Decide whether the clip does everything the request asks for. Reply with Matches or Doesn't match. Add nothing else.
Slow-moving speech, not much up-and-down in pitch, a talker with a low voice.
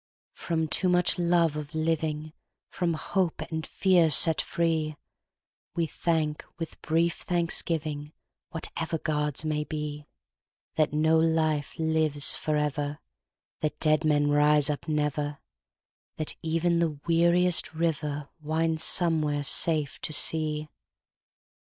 Doesn't match